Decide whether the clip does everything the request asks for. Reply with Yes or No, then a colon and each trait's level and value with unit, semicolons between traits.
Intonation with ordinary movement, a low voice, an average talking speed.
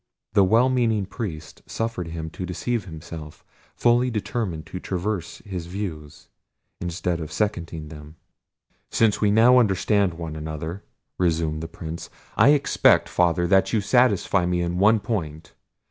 Yes: average, 4.6 semitones; very low, 90 Hz; average, 145 wpm